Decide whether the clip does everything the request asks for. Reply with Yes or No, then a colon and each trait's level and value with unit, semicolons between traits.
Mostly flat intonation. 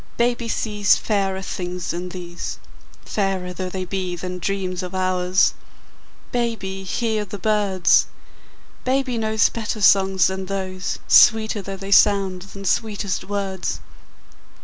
Yes: narrow, 2.2 semitones